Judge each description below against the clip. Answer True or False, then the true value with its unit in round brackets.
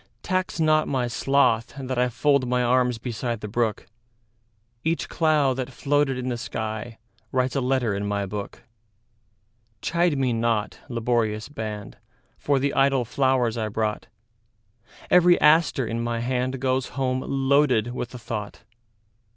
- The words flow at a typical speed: False (125 wpm)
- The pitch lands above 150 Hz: False (120 Hz)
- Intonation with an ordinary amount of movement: True (3.0 semitones)